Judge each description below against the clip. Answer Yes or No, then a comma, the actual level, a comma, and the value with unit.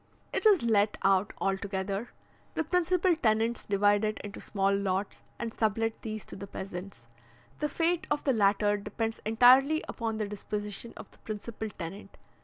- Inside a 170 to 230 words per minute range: No, average, 160 wpm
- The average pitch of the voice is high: Yes, high, 215 Hz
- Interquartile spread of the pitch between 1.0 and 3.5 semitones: Yes, average, 2.9 semitones